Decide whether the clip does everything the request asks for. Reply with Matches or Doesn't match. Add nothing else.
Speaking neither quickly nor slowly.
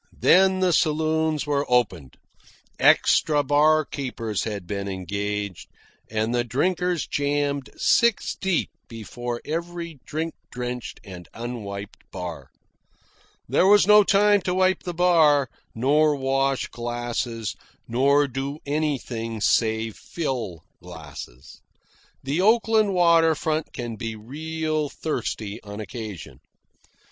Doesn't match